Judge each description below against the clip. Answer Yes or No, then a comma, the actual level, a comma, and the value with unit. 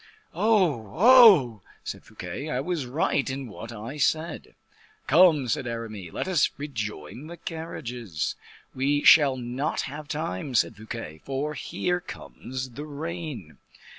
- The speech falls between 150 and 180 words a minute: No, slow, 135 wpm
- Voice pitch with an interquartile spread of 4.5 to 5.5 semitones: Yes, average, 5.2 semitones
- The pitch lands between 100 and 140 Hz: Yes, low, 135 Hz